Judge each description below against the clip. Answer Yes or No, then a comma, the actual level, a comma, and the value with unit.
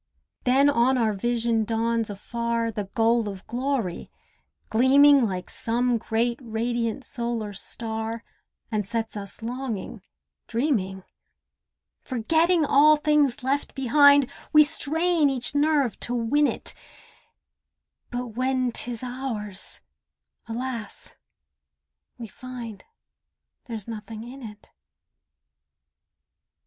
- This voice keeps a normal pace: No, slow, 100 wpm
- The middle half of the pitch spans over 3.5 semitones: No, average, 3.2 semitones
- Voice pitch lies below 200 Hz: No, high, 235 Hz